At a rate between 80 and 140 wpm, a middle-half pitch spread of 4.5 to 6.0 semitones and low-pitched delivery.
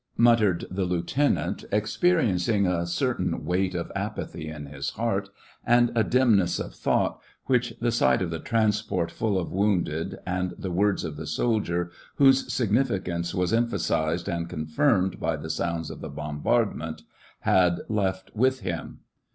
No: average, 150 wpm; average, 4.9 semitones; very low, 95 Hz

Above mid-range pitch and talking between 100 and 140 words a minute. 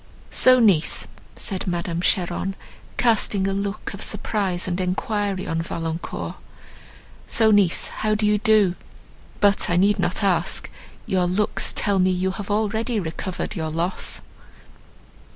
Yes: high, 195 Hz; slow, 135 wpm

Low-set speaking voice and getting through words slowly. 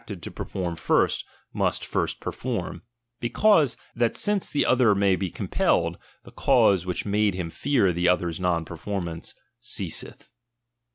No: very low, 95 Hz; average, 155 wpm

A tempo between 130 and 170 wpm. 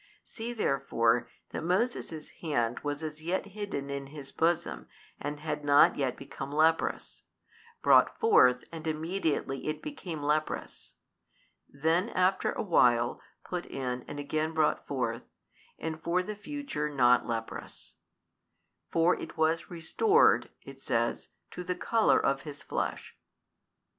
Yes: slow, 135 wpm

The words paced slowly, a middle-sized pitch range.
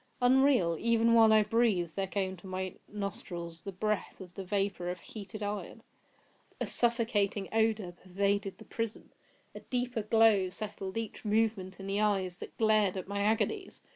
No: average, 160 wpm; average, 3.0 semitones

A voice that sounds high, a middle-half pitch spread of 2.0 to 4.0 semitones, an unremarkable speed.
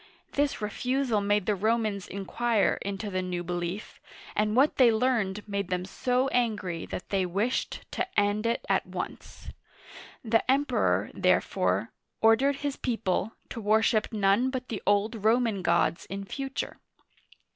Yes: high, 215 Hz; average, 3.7 semitones; average, 145 wpm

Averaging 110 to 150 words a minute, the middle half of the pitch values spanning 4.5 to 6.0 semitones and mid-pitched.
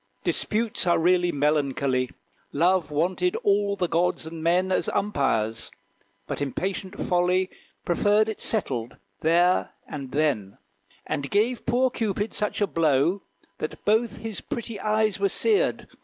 Yes: slow, 135 wpm; wide, 5.4 semitones; medium, 180 Hz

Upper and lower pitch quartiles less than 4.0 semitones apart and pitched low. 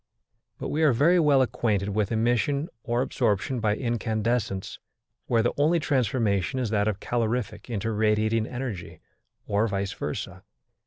Yes: average, 3.2 semitones; low, 115 Hz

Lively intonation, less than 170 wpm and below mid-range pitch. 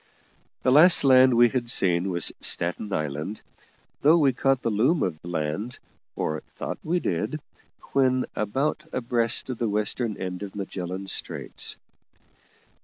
Yes: wide, 6.0 semitones; average, 140 wpm; low, 115 Hz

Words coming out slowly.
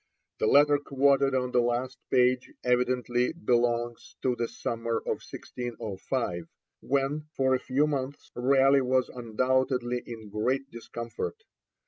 Yes: slow, 125 wpm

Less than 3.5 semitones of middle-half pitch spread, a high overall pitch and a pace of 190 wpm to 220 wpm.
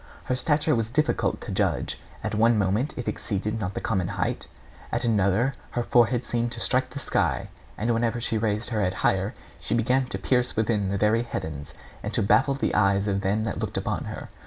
No: average, 3.1 semitones; low, 115 Hz; fast, 205 wpm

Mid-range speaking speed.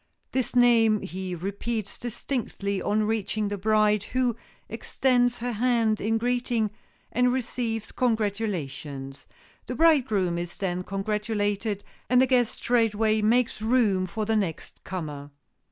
No: slow, 125 wpm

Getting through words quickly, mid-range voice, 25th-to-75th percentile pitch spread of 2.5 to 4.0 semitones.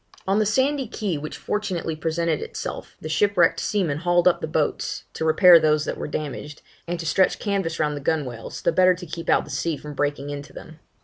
Yes: fast, 210 wpm; medium, 165 Hz; average, 3.4 semitones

